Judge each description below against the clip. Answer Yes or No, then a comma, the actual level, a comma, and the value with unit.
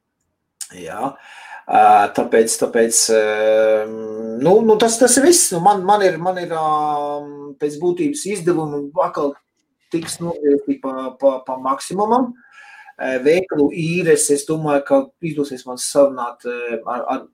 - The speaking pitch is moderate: Yes, medium, 155 Hz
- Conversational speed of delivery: No, slow, 130 wpm